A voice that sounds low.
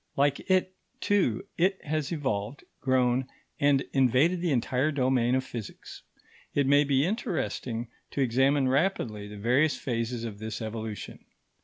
Yes: low, 130 Hz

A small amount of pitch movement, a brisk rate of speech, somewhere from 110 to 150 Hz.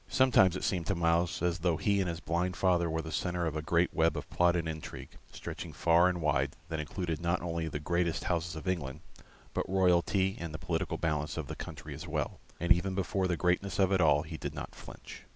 No: narrow, 2.0 semitones; fast, 230 wpm; very low, 85 Hz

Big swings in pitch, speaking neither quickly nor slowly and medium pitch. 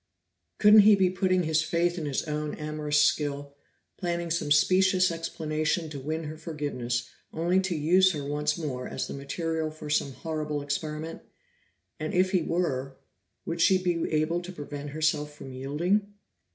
No: average, 2.8 semitones; average, 165 wpm; medium, 155 Hz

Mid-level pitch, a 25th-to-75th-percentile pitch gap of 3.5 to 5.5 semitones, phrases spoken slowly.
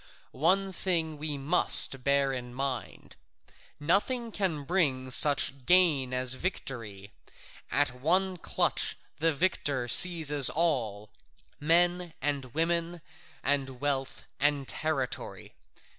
Yes: medium, 145 Hz; average, 4.6 semitones; slow, 105 wpm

